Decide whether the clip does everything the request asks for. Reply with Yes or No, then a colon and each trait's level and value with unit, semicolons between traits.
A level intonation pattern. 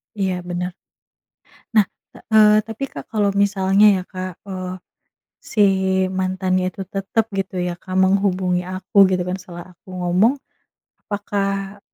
Yes: narrow, 1.8 semitones